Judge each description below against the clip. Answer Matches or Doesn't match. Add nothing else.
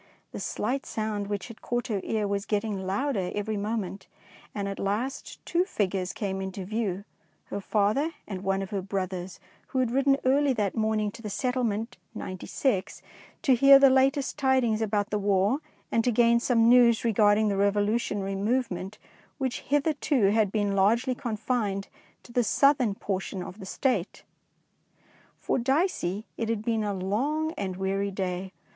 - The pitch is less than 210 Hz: Doesn't match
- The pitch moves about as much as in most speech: Matches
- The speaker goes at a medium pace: Matches